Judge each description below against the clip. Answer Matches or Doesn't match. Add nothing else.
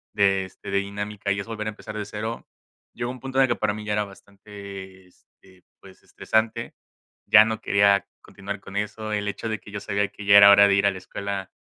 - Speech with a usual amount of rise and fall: Doesn't match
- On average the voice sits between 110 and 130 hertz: Doesn't match